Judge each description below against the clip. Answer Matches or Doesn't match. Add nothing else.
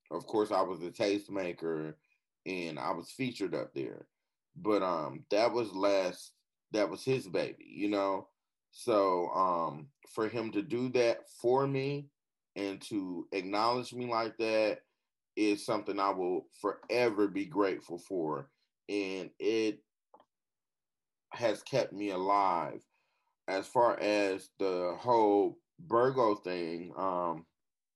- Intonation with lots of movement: Doesn't match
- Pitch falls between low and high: Doesn't match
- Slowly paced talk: Matches